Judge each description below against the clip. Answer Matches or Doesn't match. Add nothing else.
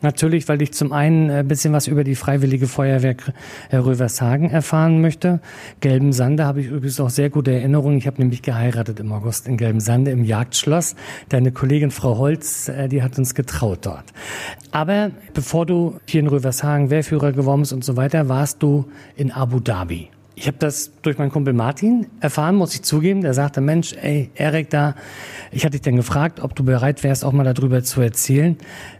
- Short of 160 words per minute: Doesn't match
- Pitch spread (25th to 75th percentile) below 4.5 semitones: Matches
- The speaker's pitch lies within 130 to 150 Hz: Matches